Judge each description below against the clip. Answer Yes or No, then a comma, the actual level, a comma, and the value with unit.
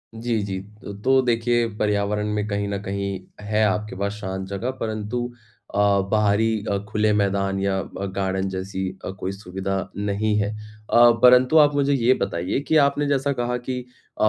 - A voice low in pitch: Yes, low, 105 Hz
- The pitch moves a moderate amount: Yes, average, 3.4 semitones